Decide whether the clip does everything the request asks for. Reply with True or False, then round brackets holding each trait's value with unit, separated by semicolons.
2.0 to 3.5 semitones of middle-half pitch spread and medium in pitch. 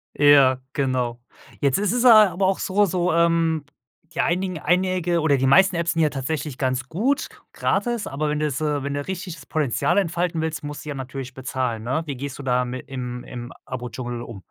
False (5.0 semitones; 145 Hz)